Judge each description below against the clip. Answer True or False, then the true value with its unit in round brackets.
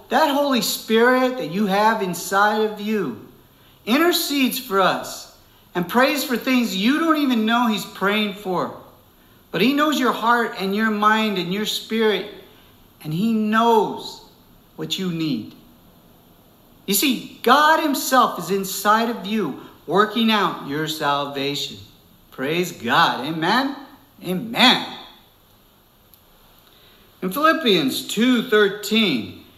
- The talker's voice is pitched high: True (215 Hz)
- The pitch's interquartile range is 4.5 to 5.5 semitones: True (5.1 semitones)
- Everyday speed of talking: False (120 wpm)